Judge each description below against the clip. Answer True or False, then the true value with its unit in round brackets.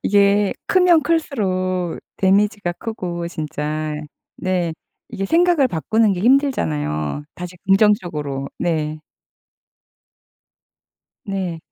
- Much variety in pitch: False (4.9 semitones)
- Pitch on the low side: False (185 Hz)